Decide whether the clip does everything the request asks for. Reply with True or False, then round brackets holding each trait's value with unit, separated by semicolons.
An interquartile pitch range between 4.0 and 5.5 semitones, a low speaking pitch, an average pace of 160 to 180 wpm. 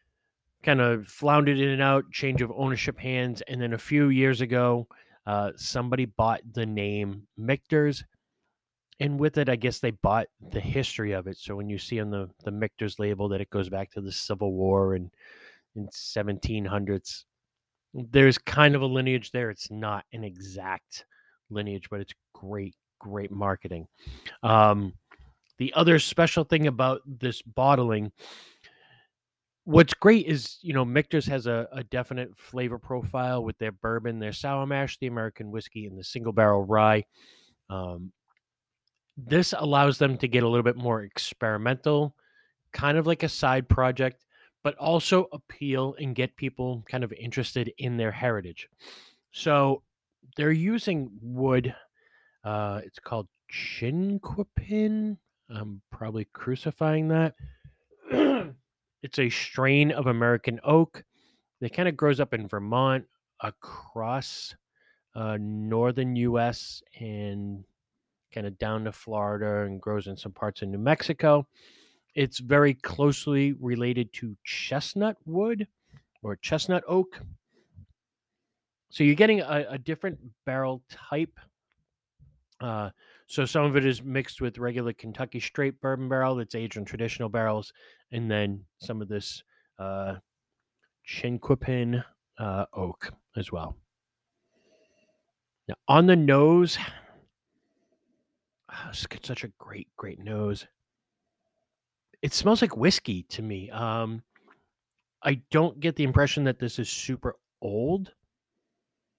False (5.0 semitones; 125 Hz; 135 wpm)